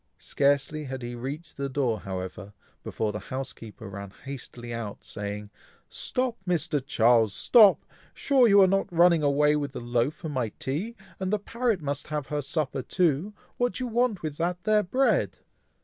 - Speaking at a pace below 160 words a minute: No, average, 175 wpm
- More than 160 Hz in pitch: No, medium, 145 Hz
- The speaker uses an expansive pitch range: Yes, wide, 7.4 semitones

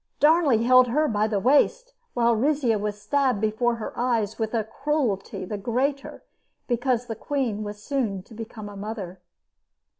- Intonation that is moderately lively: Yes, average, 4.0 semitones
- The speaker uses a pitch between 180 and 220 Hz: No, high, 230 Hz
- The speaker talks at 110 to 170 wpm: Yes, average, 160 wpm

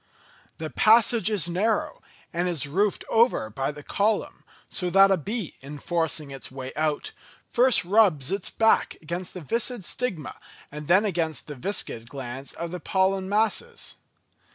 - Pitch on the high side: No, medium, 180 Hz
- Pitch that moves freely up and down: Yes, wide, 6.0 semitones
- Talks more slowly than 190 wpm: Yes, average, 155 wpm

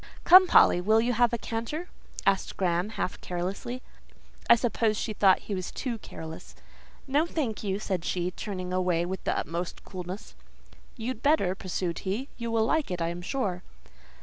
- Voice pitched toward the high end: Yes, high, 200 Hz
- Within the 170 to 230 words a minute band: Yes, average, 175 wpm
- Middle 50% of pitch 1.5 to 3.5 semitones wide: No, average, 4.6 semitones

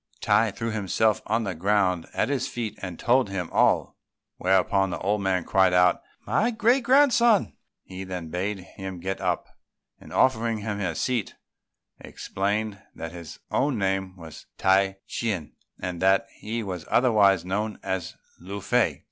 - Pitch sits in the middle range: No, low, 100 Hz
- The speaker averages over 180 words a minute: No, average, 155 wpm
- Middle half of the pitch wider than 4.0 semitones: No, average, 3.4 semitones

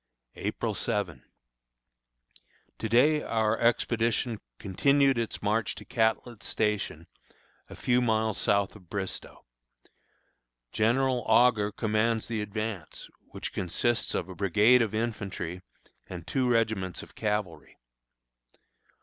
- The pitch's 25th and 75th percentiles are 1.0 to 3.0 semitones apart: Yes, narrow, 2.6 semitones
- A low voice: Yes, low, 110 Hz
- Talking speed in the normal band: No, slow, 110 wpm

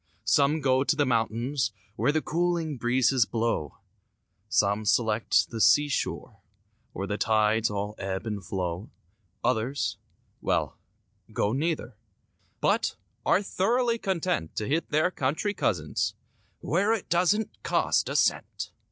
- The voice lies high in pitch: No, low, 130 Hz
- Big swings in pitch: Yes, wide, 6.9 semitones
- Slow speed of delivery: Yes, slow, 125 wpm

